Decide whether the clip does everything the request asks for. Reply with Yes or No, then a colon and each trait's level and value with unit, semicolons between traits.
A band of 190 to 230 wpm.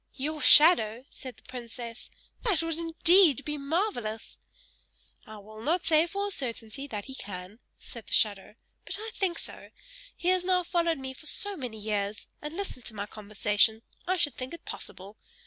No: average, 180 wpm